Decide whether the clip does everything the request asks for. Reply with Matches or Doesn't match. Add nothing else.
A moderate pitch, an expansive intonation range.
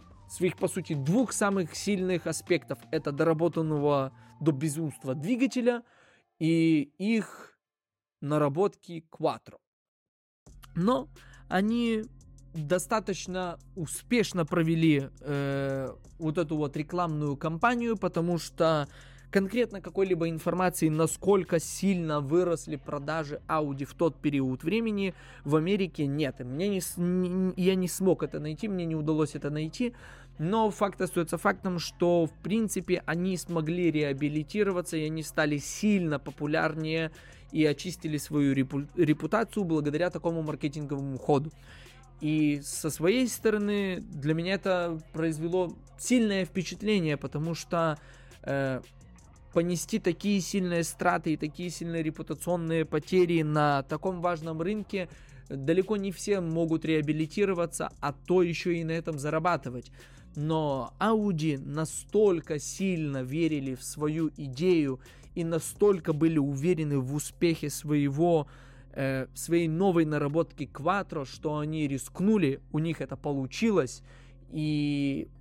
Doesn't match